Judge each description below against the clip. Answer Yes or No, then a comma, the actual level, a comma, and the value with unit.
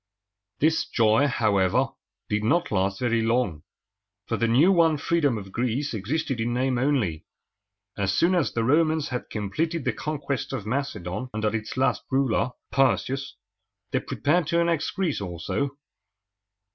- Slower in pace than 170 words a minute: Yes, average, 145 wpm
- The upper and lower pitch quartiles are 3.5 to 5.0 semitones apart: No, wide, 5.5 semitones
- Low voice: Yes, low, 125 Hz